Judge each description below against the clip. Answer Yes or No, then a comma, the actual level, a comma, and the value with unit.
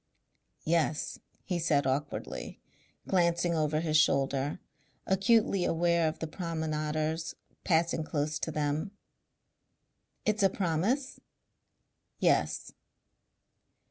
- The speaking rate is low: Yes, slow, 90 wpm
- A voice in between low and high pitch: Yes, medium, 160 Hz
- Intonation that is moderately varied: No, narrow, 2.3 semitones